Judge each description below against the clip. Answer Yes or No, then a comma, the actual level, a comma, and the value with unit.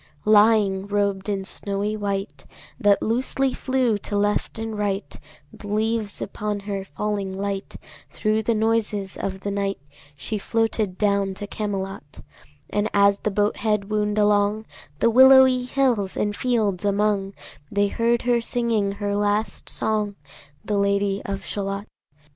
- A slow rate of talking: No, average, 150 wpm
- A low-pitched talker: No, high, 205 Hz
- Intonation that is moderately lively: No, narrow, 1.6 semitones